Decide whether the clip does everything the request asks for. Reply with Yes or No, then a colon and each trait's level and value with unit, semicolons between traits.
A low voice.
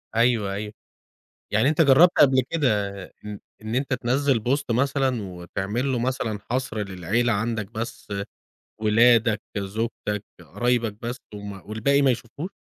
Yes: low, 115 Hz